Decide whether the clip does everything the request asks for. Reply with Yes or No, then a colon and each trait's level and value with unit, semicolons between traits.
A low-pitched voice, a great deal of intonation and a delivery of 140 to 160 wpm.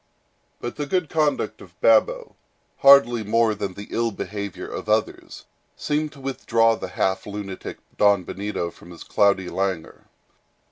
Yes: low, 105 Hz; wide, 5.8 semitones; average, 145 wpm